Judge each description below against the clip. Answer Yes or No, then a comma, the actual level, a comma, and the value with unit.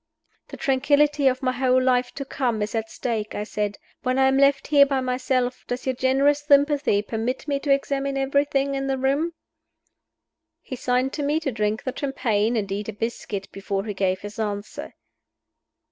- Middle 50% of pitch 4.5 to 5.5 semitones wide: No, average, 4.0 semitones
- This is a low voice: No, very high, 255 Hz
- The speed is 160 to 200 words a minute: Yes, average, 185 wpm